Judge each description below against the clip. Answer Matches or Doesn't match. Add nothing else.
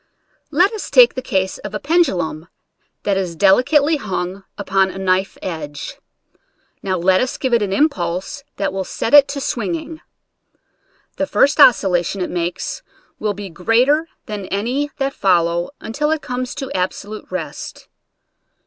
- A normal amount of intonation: Doesn't match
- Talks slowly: Doesn't match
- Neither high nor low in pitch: Doesn't match